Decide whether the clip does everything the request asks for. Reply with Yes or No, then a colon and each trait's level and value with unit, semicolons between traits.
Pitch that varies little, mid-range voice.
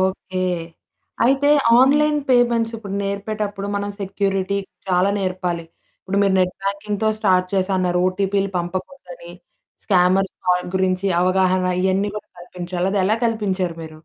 No: narrow, 2.0 semitones; high, 195 Hz